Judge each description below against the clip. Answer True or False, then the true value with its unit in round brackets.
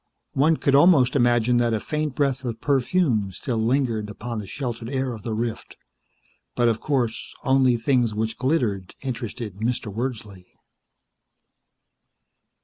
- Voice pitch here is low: True (120 Hz)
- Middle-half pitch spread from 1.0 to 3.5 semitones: True (3.2 semitones)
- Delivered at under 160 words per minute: True (140 wpm)